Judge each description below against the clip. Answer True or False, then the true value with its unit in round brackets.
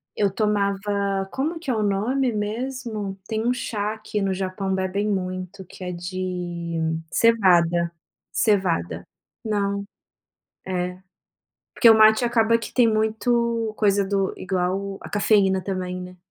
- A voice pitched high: True (200 Hz)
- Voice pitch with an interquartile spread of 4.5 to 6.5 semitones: False (2.9 semitones)